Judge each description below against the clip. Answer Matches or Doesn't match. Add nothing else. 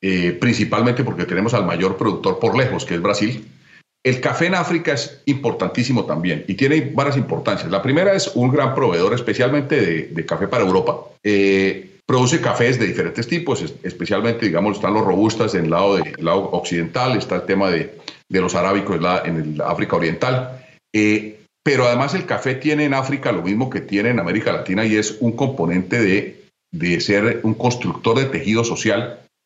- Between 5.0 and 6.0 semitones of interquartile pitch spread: Matches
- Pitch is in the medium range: Doesn't match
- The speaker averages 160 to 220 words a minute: Matches